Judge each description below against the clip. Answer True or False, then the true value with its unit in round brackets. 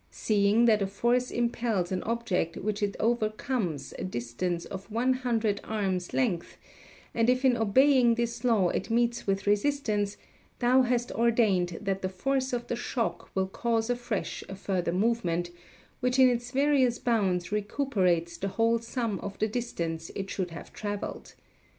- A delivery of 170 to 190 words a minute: False (160 wpm)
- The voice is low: False (220 Hz)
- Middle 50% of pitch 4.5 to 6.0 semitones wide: False (4.0 semitones)